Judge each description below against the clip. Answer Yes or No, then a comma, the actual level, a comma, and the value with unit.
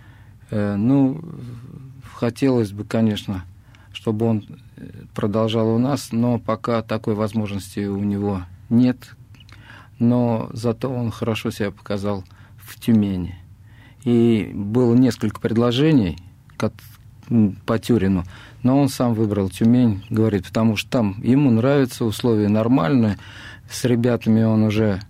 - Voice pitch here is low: Yes, low, 110 Hz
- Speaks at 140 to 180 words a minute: No, slow, 110 wpm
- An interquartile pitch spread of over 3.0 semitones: No, narrow, 2.6 semitones